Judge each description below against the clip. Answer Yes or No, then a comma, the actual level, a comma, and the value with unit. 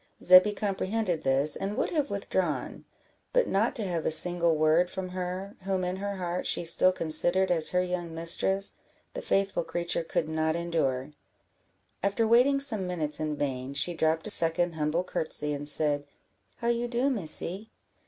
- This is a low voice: No, medium, 180 Hz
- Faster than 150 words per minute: Yes, average, 170 wpm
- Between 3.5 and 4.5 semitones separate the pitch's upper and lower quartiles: Yes, average, 3.8 semitones